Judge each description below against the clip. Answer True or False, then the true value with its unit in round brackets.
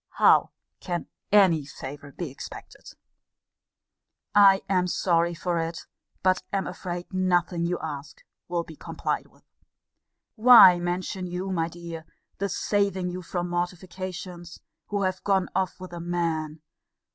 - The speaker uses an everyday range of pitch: False (1.8 semitones)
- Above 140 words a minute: False (135 wpm)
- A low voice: False (175 Hz)